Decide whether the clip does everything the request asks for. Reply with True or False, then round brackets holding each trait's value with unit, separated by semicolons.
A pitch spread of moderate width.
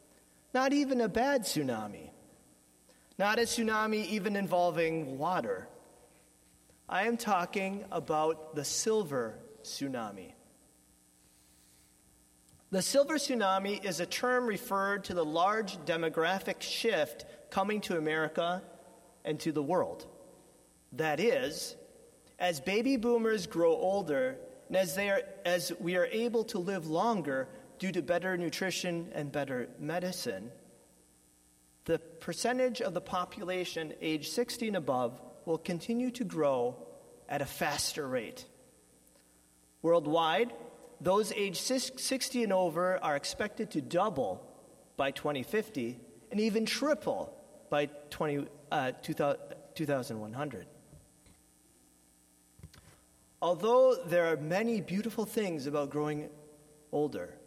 False (6.8 semitones)